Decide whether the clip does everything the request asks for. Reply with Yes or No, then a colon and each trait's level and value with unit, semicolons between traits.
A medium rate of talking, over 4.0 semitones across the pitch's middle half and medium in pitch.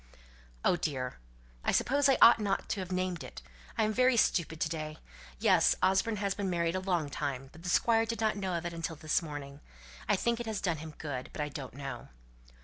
No: fast, 220 wpm; wide, 5.4 semitones; medium, 175 Hz